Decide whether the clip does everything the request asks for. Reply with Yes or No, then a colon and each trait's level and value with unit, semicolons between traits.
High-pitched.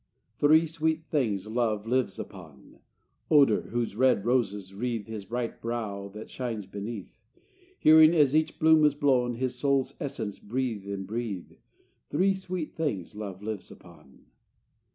No: low, 120 Hz